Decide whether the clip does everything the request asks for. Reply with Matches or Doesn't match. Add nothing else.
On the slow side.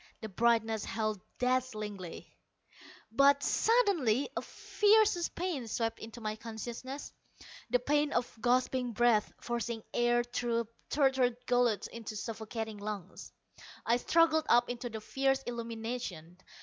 Matches